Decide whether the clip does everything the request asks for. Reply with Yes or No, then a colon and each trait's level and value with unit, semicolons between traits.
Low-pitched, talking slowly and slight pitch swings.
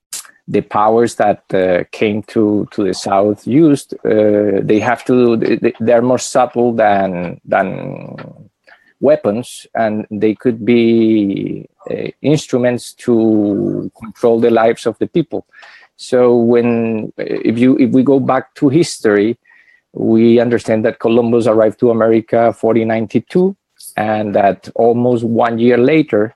Yes: low, 115 Hz; slow, 130 wpm; narrow, 2.2 semitones